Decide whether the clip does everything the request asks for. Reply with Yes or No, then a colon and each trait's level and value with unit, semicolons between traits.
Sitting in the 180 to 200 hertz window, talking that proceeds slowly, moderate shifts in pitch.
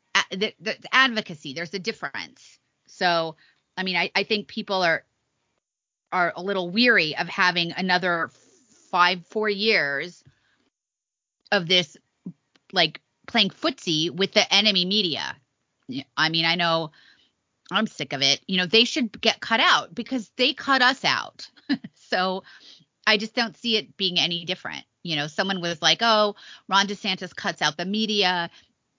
No: high, 190 Hz; average, 155 wpm; average, 4.1 semitones